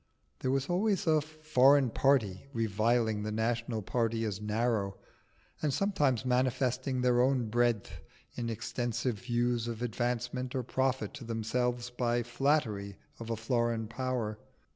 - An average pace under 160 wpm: Yes, slow, 135 wpm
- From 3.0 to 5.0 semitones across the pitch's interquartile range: No, narrow, 2.4 semitones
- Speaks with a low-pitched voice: Yes, low, 120 Hz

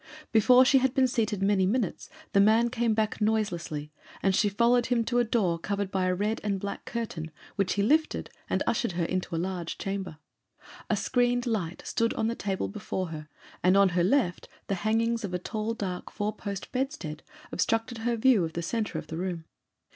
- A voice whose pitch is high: Yes, high, 205 Hz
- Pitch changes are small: No, average, 4.1 semitones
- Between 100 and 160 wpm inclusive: No, average, 200 wpm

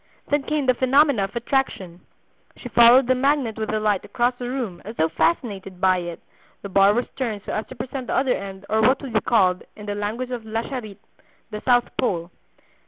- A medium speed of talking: No, fast, 210 wpm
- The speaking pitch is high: Yes, high, 225 Hz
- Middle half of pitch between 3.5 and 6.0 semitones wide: Yes, average, 4.2 semitones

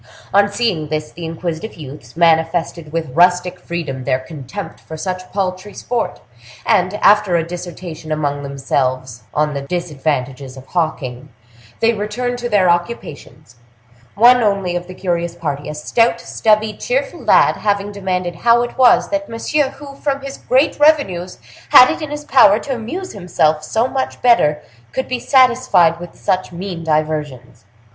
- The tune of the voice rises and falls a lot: Yes, wide, 6.7 semitones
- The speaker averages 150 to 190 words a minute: Yes, average, 155 wpm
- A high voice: No, medium, 180 Hz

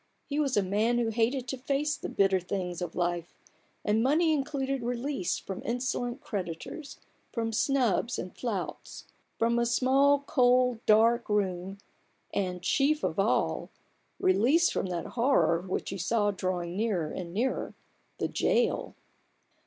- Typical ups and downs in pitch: No, wide, 5.9 semitones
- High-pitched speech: Yes, high, 230 Hz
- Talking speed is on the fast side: No, average, 145 wpm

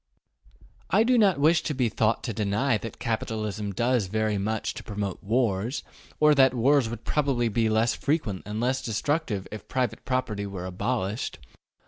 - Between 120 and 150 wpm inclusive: No, average, 165 wpm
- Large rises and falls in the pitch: No, average, 4.0 semitones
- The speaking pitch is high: No, low, 115 Hz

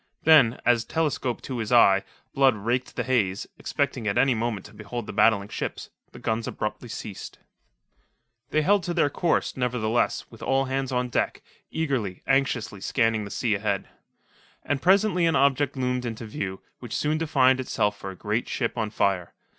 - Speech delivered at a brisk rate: No, average, 175 wpm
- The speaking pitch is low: Yes, low, 120 Hz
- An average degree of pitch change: Yes, average, 4.1 semitones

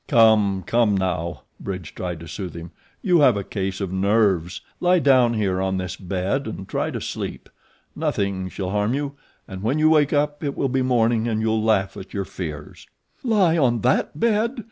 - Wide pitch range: Yes, wide, 6.1 semitones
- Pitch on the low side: Yes, low, 110 Hz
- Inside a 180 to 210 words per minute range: Yes, average, 190 wpm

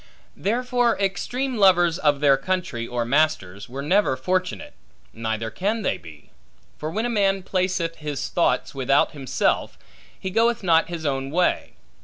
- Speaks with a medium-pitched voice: Yes, medium, 165 Hz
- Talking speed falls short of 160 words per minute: Yes, average, 150 wpm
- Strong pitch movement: Yes, wide, 6.3 semitones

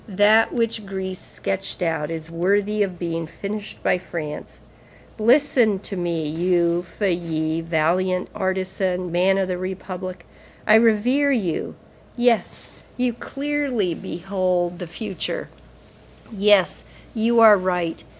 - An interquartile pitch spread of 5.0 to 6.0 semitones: No, average, 3.5 semitones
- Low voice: No, medium, 185 Hz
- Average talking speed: No, slow, 120 wpm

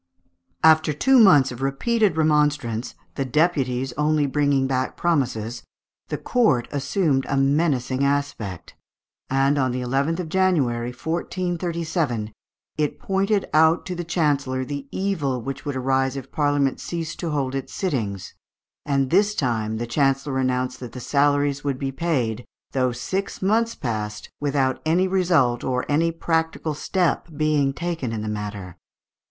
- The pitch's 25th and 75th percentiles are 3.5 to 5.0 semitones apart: Yes, average, 4.1 semitones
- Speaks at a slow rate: No, average, 145 wpm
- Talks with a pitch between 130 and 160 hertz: Yes, medium, 140 Hz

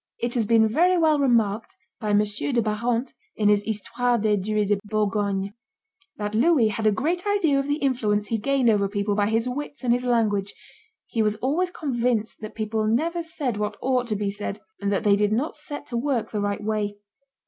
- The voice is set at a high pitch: Yes, high, 220 Hz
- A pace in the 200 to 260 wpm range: Yes, fast, 205 wpm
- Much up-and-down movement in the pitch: No, average, 3.8 semitones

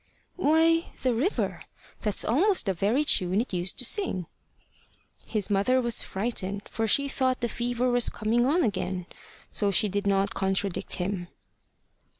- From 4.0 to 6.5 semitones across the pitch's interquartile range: Yes, average, 4.7 semitones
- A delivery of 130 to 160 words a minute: Yes, average, 150 wpm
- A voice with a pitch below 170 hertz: No, high, 225 Hz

